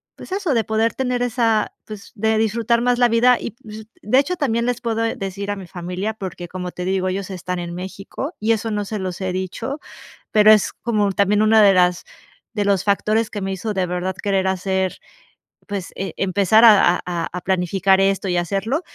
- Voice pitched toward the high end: Yes, high, 200 Hz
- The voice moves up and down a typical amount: Yes, average, 3.1 semitones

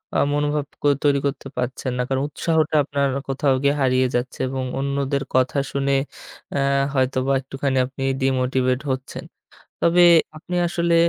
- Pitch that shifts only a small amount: Yes, narrow, 1.8 semitones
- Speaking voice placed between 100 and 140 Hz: Yes, low, 135 Hz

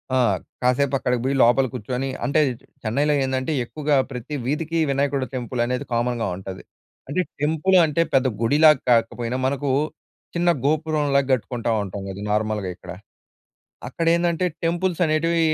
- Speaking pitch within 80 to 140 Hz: Yes, low, 135 Hz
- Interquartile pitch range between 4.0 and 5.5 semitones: Yes, average, 4.3 semitones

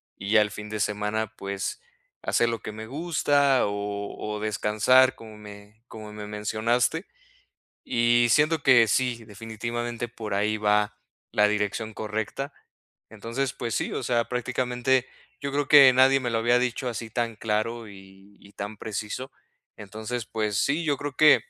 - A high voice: No, low, 115 Hz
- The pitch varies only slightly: No, average, 3.1 semitones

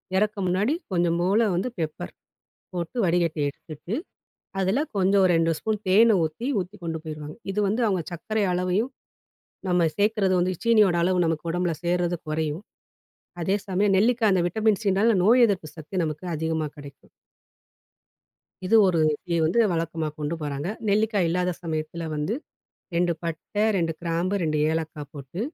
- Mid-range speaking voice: Yes, medium, 175 Hz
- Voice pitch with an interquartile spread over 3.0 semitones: Yes, average, 3.8 semitones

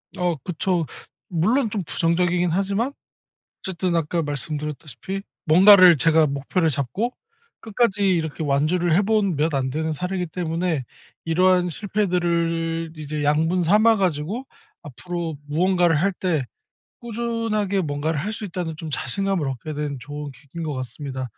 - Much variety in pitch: No, average, 4.0 semitones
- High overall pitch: No, medium, 170 Hz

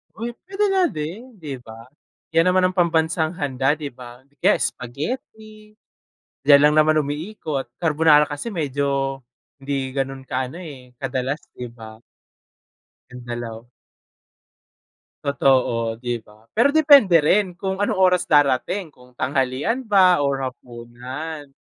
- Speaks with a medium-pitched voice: Yes, medium, 145 Hz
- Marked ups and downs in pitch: Yes, wide, 5.7 semitones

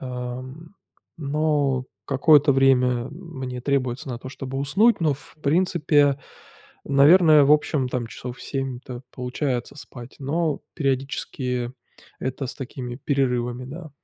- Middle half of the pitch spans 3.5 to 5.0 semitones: No, average, 2.7 semitones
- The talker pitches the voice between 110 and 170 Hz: Yes, low, 135 Hz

